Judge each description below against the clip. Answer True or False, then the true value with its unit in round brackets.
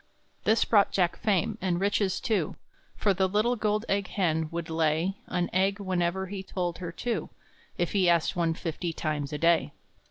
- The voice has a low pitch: False (185 Hz)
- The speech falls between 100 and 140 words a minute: False (180 wpm)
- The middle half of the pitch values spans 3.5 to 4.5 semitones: False (3.1 semitones)